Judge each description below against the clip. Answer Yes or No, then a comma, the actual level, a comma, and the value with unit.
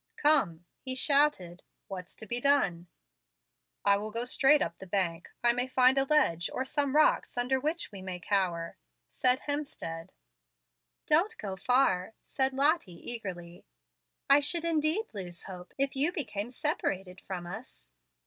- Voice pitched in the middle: No, high, 240 Hz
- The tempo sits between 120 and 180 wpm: Yes, average, 150 wpm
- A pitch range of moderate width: No, wide, 7.6 semitones